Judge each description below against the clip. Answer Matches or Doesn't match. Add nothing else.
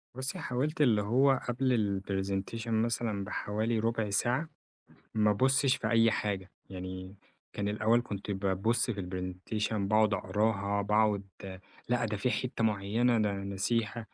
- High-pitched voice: Doesn't match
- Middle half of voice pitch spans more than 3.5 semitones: Doesn't match